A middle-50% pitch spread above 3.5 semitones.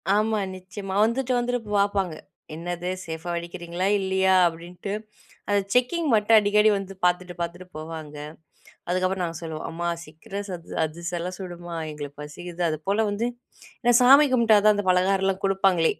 No: average, 3.1 semitones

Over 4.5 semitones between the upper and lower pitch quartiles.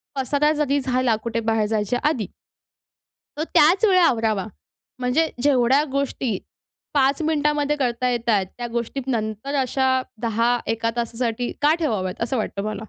No: average, 3.9 semitones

